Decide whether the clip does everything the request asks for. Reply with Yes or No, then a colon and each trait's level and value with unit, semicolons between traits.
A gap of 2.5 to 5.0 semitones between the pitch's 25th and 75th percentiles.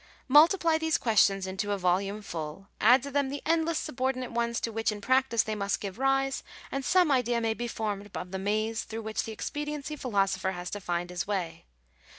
No: wide, 5.4 semitones